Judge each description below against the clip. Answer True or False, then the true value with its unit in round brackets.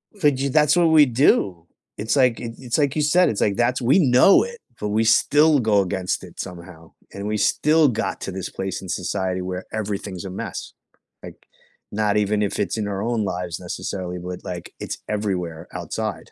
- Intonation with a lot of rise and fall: True (6.0 semitones)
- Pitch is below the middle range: True (105 Hz)